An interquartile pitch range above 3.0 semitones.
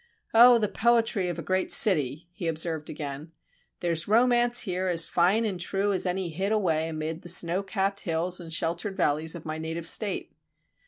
Yes: average, 3.7 semitones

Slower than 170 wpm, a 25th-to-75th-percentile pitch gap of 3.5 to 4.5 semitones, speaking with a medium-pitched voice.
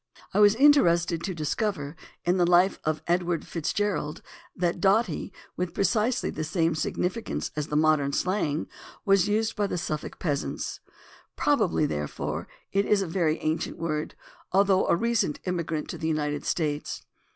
Yes: average, 155 wpm; average, 4.2 semitones; medium, 175 Hz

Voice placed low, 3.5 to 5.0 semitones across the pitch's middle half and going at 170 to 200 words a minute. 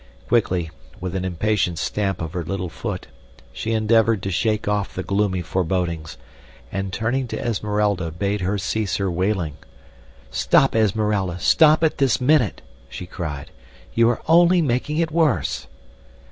No: low, 100 Hz; average, 4.1 semitones; average, 145 wpm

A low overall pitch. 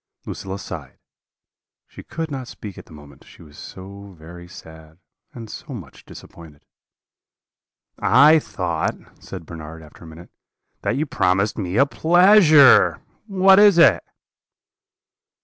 Yes: very low, 95 Hz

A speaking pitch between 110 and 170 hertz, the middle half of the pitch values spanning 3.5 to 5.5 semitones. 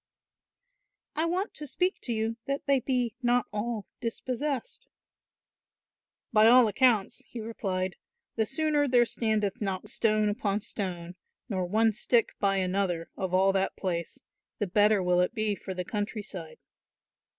No: high, 215 Hz; average, 4.0 semitones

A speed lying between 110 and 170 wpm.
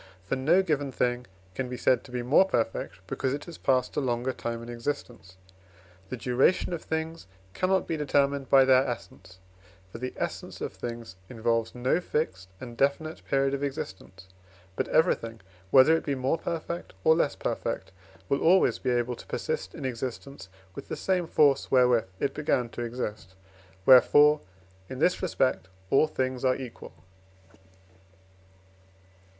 Yes: average, 160 wpm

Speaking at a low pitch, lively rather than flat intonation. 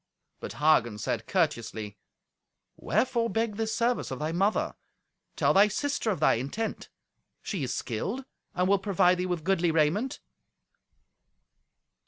No: medium, 185 Hz; wide, 6.5 semitones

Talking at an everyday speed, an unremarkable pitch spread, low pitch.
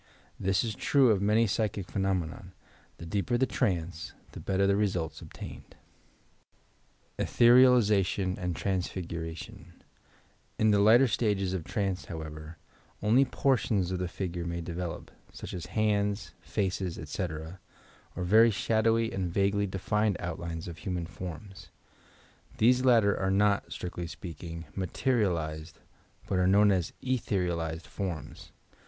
Yes: average, 150 wpm; average, 3.6 semitones; very low, 95 Hz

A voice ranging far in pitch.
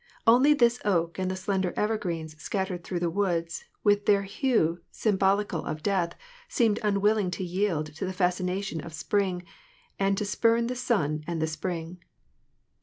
No: average, 3.3 semitones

